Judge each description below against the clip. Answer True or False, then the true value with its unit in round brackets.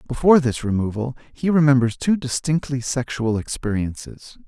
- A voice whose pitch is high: False (130 Hz)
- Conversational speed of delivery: False (120 wpm)